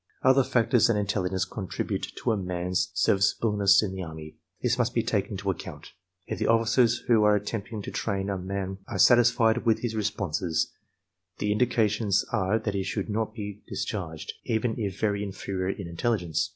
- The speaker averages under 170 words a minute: No, average, 175 wpm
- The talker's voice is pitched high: No, low, 105 Hz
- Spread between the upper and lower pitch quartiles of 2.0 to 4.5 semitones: Yes, average, 2.9 semitones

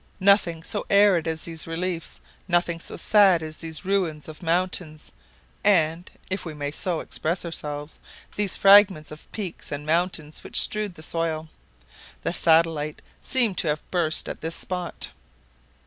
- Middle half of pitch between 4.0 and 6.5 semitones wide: No, average, 2.9 semitones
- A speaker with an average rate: Yes, average, 150 wpm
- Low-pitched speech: No, medium, 165 Hz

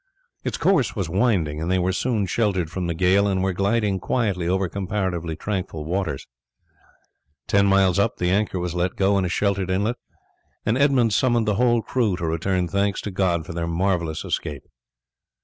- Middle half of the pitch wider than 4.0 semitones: No, average, 2.8 semitones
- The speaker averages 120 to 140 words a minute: No, average, 185 wpm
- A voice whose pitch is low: Yes, very low, 95 Hz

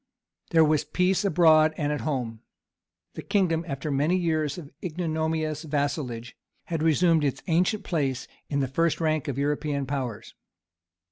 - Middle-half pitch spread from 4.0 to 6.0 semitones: No, average, 2.7 semitones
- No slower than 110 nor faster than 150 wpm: Yes, average, 145 wpm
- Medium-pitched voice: Yes, medium, 155 Hz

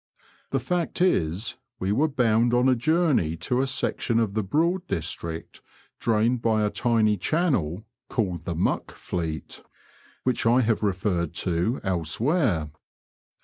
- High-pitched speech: No, low, 110 Hz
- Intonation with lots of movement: Yes, wide, 6.5 semitones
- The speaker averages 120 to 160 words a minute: Yes, average, 145 wpm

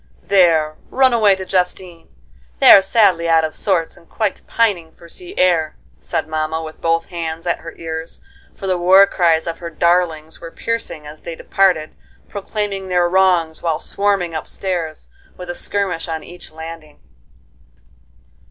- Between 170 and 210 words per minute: No, average, 160 wpm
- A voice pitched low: No, medium, 170 Hz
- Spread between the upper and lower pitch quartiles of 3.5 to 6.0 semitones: No, average, 2.9 semitones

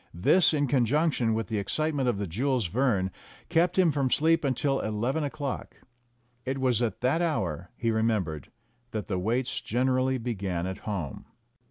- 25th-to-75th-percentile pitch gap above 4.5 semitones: Yes, average, 5.1 semitones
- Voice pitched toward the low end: Yes, low, 125 Hz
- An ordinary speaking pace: Yes, average, 165 wpm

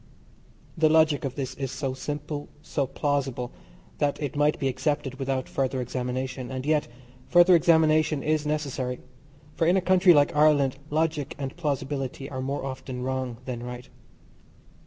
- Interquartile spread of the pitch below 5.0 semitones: Yes, average, 2.7 semitones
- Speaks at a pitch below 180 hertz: Yes, medium, 140 Hz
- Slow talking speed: No, average, 155 wpm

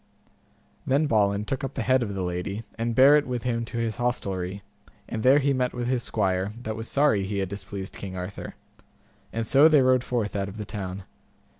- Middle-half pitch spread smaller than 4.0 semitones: No, average, 4.5 semitones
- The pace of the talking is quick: Yes, fast, 210 wpm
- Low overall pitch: Yes, low, 110 Hz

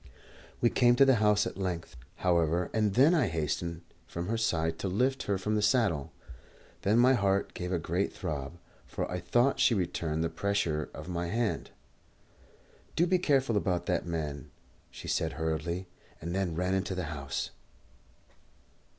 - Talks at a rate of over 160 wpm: Yes, average, 170 wpm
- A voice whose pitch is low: Yes, very low, 95 Hz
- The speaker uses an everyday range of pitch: Yes, average, 5.0 semitones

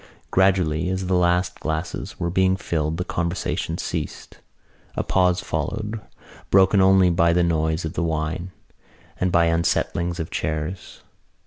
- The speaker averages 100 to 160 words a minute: Yes, average, 140 wpm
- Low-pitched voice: Yes, very low, 85 Hz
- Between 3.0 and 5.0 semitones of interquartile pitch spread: No, narrow, 2.4 semitones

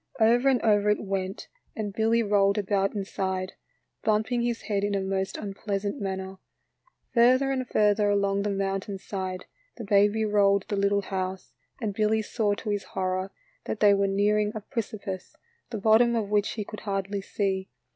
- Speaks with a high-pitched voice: Yes, high, 205 Hz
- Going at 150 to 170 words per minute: Yes, average, 165 wpm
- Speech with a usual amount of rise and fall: No, narrow, 1.8 semitones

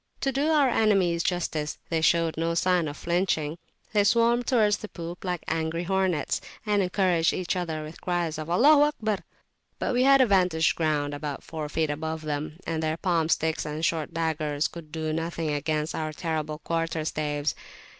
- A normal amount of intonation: Yes, average, 3.1 semitones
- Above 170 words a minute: Yes, average, 180 wpm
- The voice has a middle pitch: Yes, medium, 165 Hz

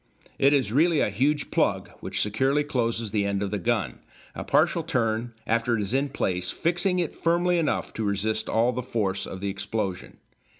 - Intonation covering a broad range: Yes, wide, 5.9 semitones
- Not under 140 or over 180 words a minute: No, average, 195 wpm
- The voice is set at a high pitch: No, low, 115 Hz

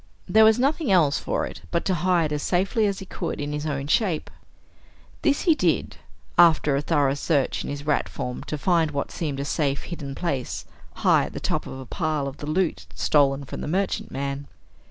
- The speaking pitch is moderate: Yes, medium, 150 Hz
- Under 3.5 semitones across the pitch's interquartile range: No, average, 4.3 semitones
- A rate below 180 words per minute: No, fast, 205 wpm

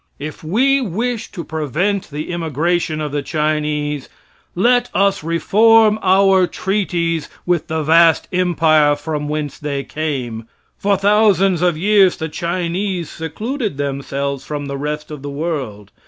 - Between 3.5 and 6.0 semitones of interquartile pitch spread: Yes, average, 4.6 semitones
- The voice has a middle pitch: Yes, medium, 165 Hz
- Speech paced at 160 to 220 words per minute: No, average, 140 wpm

